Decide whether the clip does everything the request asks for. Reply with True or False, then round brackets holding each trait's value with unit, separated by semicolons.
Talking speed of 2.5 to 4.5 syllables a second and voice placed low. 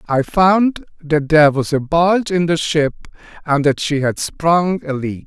False (4.3 syllables/s; 155 Hz)